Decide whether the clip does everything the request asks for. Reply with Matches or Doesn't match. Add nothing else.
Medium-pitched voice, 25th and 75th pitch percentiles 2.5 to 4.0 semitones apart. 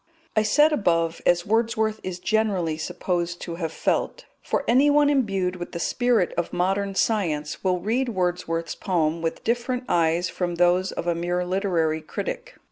Doesn't match